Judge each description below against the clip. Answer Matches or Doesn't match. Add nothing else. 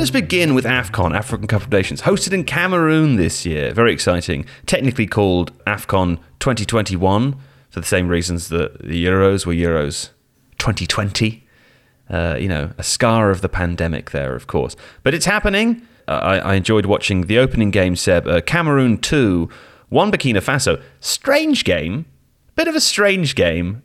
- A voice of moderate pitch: Doesn't match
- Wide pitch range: Matches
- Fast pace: Doesn't match